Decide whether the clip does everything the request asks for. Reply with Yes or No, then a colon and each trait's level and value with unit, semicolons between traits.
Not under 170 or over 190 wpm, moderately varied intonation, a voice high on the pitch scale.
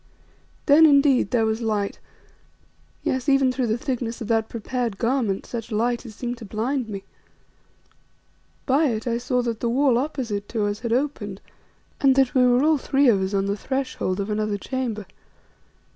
Yes: average, 175 wpm; average, 3.5 semitones; high, 240 Hz